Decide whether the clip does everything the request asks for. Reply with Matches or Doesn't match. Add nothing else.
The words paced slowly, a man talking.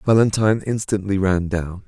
Matches